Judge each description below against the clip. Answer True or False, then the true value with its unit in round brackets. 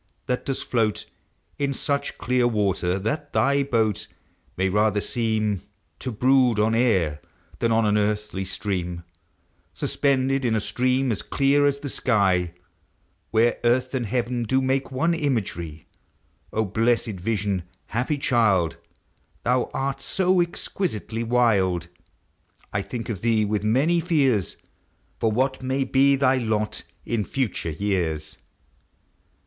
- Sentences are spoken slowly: True (130 wpm)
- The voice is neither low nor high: False (115 Hz)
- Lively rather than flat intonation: False (4.3 semitones)